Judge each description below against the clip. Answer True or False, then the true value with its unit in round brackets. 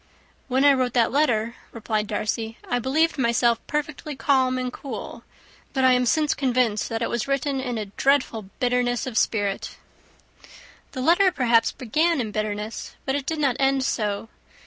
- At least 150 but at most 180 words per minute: True (170 wpm)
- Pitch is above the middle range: True (250 Hz)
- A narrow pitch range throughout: False (3.4 semitones)